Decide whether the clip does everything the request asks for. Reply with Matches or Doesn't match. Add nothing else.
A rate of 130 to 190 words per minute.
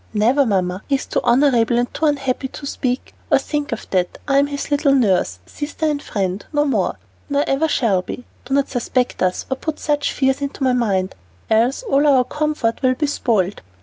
Doesn't match